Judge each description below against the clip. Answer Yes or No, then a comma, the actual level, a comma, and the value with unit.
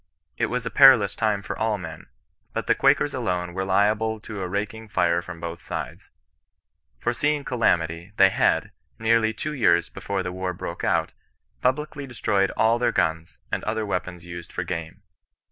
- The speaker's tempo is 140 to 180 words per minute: Yes, average, 175 wpm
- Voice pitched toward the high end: No, low, 100 Hz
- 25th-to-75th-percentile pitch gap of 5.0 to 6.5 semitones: No, average, 4.3 semitones